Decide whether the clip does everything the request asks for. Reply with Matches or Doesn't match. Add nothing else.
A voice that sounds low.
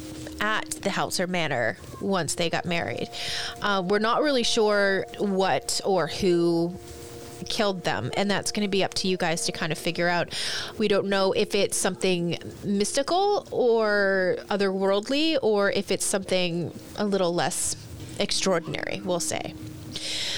Doesn't match